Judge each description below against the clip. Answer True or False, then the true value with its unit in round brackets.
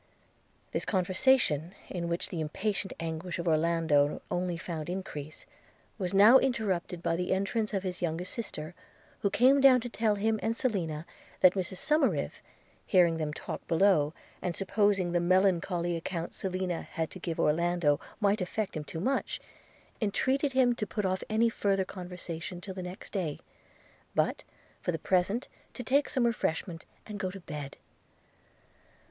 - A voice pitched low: False (185 Hz)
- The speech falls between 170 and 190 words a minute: False (155 wpm)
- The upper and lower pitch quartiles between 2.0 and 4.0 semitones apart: True (3.7 semitones)